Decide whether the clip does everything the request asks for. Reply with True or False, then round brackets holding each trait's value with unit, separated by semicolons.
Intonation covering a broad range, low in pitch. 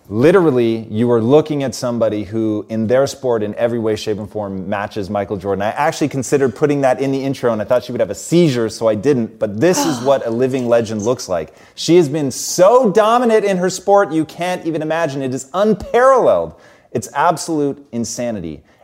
True (6.0 semitones; 130 Hz)